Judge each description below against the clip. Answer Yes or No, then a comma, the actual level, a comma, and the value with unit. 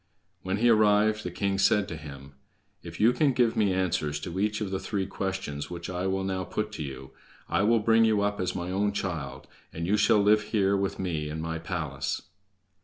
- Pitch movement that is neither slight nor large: Yes, average, 3.8 semitones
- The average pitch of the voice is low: Yes, very low, 95 Hz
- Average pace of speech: No, fast, 215 wpm